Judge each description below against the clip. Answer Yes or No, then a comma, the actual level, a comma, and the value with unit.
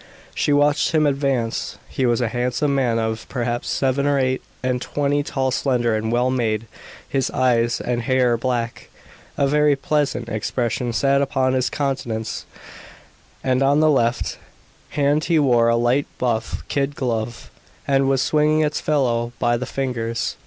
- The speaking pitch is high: No, low, 130 Hz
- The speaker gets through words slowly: No, average, 160 wpm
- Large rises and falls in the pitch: No, average, 3.0 semitones